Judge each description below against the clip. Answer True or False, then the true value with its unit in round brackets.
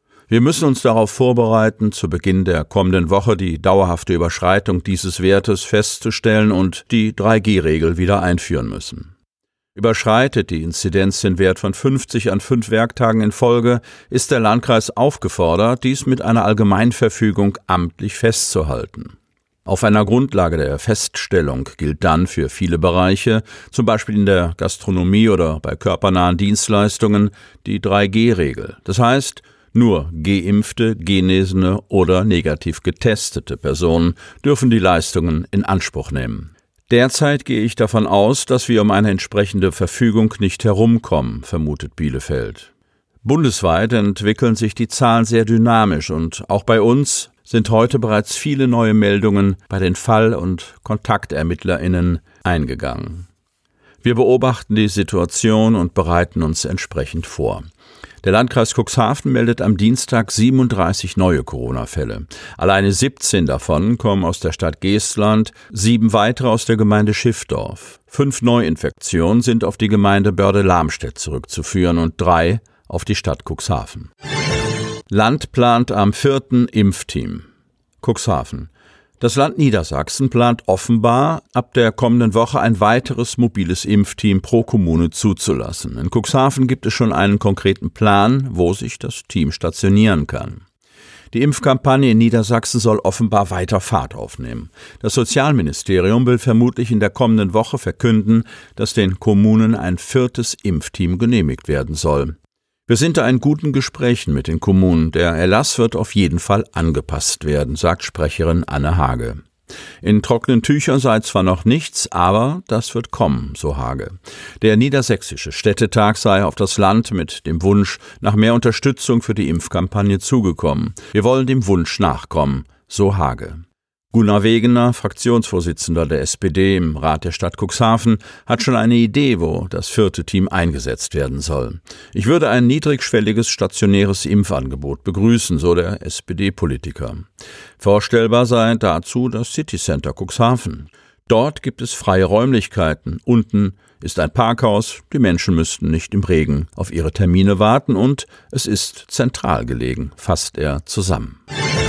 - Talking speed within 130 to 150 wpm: True (140 wpm)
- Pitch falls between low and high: False (105 Hz)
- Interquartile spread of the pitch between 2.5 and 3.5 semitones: False (4.5 semitones)